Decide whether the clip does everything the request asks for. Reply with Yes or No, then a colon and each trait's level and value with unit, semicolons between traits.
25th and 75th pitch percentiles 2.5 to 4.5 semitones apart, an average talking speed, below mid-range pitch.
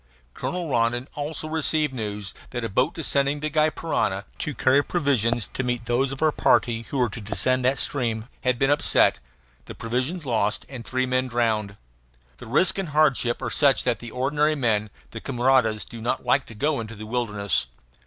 Yes: average, 4.0 semitones; average, 190 wpm; low, 125 Hz